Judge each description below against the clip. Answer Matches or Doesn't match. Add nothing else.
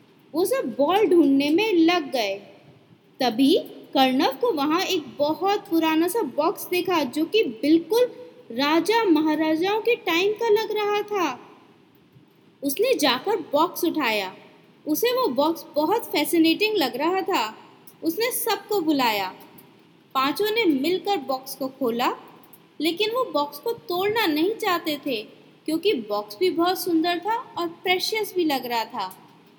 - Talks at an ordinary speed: Matches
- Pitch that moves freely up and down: Matches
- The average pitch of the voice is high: Matches